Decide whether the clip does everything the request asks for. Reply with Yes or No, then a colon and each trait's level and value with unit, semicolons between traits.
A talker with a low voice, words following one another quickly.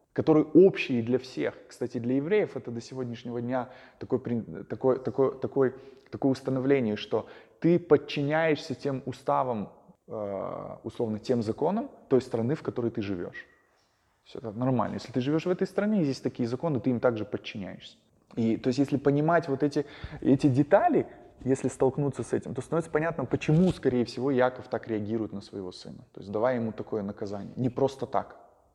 Yes: low, 130 Hz; fast, 170 wpm